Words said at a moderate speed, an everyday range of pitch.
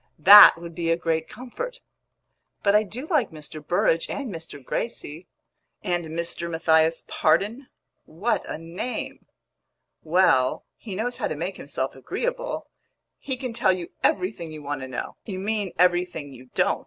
Yes: average, 155 wpm; average, 5.0 semitones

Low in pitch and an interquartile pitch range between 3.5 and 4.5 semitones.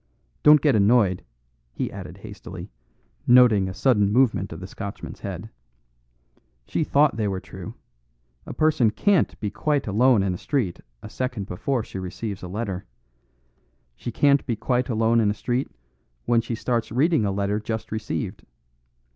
Yes: low, 110 Hz; average, 4.2 semitones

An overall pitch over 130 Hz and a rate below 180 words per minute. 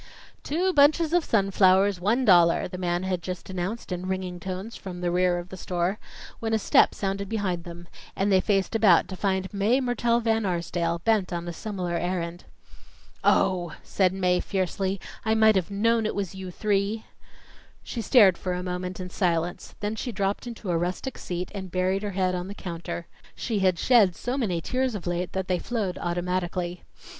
No: high, 190 Hz; average, 190 wpm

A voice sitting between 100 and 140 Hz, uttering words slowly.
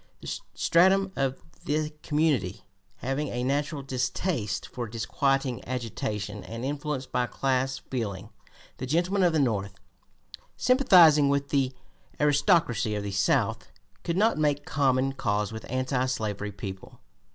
Yes: low, 135 Hz; slow, 130 wpm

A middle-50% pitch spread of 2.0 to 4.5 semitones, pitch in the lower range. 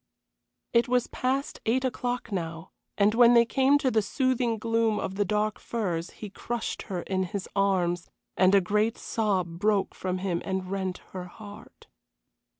No: average, 3.9 semitones; high, 205 Hz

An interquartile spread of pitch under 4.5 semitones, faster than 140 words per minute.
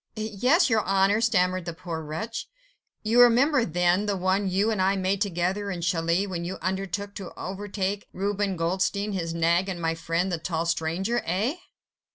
Yes: average, 3.0 semitones; average, 175 wpm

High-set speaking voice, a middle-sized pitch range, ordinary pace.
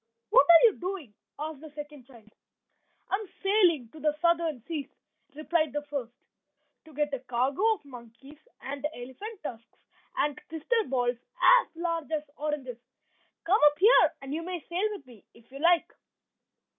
Yes: very high, 300 Hz; average, 4.3 semitones; average, 165 wpm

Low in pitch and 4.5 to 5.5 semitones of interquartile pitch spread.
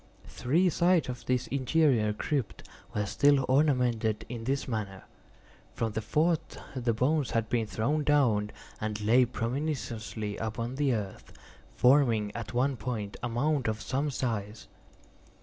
No: low, 120 Hz; average, 4.1 semitones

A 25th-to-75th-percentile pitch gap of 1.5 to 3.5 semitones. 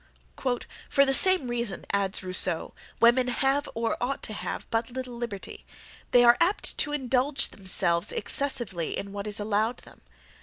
No: average, 4.7 semitones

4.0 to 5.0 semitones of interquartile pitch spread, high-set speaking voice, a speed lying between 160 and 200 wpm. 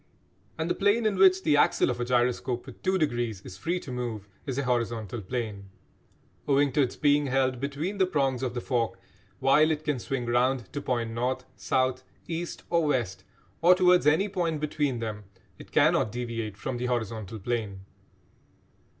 No: average, 4.3 semitones; low, 130 Hz; average, 180 wpm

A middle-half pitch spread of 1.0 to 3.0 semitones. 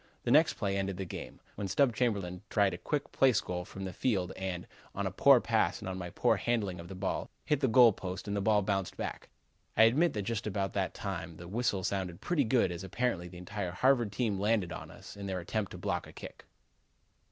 No: average, 3.8 semitones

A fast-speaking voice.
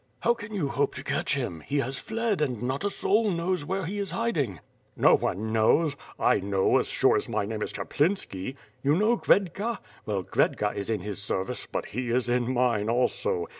Yes: fast, 210 wpm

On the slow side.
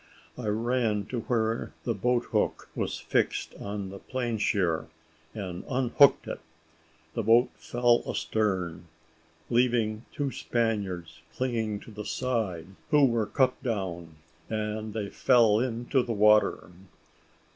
Yes: slow, 125 wpm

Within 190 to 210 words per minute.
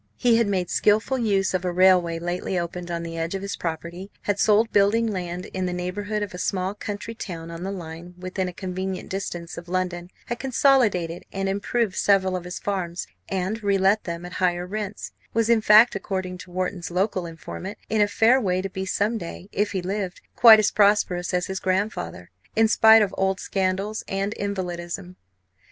Yes: average, 195 wpm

